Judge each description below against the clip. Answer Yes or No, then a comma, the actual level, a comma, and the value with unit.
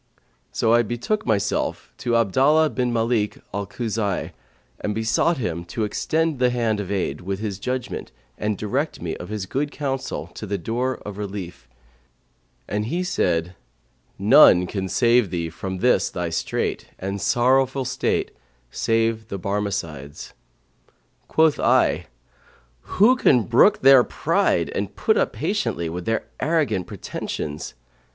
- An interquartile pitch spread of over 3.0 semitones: Yes, average, 4.9 semitones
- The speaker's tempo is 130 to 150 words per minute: Yes, average, 140 wpm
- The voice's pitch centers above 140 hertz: No, low, 110 Hz